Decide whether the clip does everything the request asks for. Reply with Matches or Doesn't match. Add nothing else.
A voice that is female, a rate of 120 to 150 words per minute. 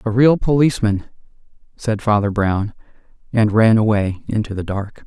Doesn't match